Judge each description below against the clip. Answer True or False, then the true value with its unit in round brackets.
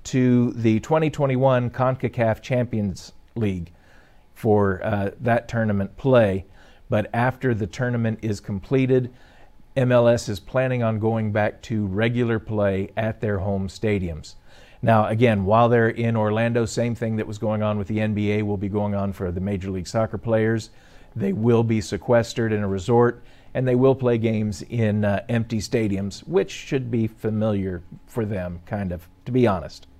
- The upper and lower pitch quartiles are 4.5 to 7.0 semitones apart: False (2.9 semitones)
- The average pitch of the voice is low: True (110 Hz)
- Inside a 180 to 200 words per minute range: False (165 wpm)